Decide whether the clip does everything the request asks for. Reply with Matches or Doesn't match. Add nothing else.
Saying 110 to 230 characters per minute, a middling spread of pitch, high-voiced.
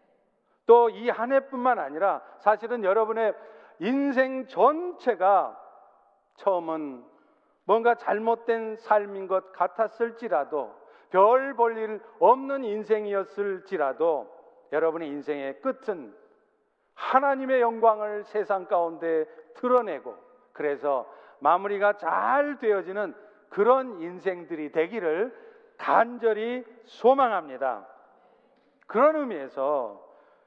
Matches